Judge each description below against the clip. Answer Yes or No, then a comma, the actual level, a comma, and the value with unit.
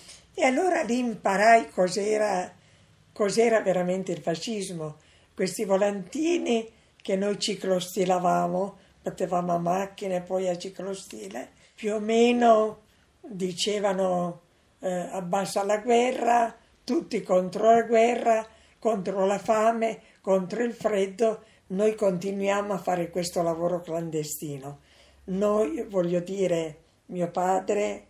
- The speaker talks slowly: Yes, slow, 110 wpm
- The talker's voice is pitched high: Yes, high, 195 Hz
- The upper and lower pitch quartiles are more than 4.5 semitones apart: No, average, 3.4 semitones